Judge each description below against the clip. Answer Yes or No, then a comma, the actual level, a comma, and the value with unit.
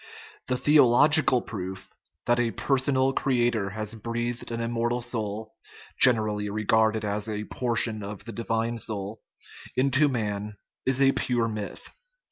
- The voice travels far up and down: No, narrow, 2.6 semitones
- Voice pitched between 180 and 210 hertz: No, low, 115 Hz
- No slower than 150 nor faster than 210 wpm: No, slow, 135 wpm